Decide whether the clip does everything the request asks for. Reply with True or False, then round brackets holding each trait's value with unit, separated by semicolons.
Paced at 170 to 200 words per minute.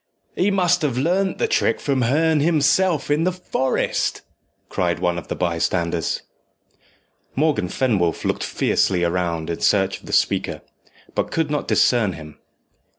False (150 wpm)